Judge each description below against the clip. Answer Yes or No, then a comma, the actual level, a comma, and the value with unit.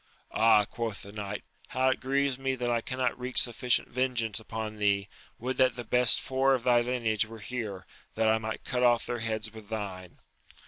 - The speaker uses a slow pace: No, average, 195 wpm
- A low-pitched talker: Yes, low, 115 Hz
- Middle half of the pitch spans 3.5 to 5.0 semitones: No, narrow, 2.6 semitones